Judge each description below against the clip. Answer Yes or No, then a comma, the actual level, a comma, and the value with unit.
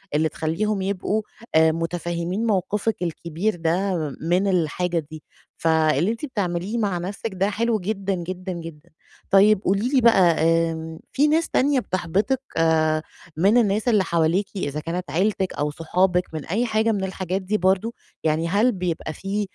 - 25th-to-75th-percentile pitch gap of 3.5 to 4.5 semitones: Yes, average, 4.0 semitones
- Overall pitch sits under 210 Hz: Yes, medium, 185 Hz